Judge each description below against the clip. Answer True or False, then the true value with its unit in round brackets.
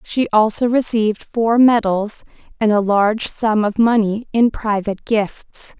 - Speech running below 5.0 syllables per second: True (4.2 syllables/s)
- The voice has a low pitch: False (215 Hz)